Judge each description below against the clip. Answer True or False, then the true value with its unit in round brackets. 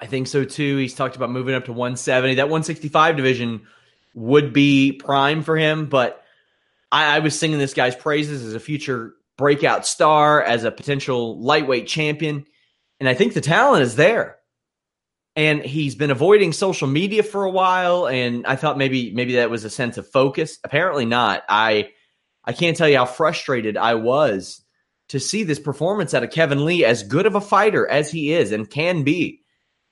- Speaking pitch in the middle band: True (145 Hz)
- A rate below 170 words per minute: False (190 wpm)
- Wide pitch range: False (3.5 semitones)